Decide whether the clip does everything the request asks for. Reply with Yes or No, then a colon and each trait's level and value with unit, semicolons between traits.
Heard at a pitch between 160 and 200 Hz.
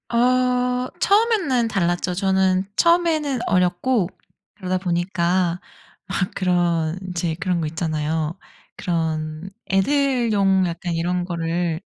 Yes: medium, 185 Hz